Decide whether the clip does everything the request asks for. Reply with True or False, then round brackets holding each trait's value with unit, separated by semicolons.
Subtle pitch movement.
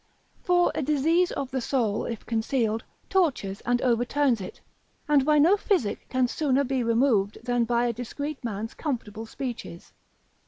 False (4.1 semitones)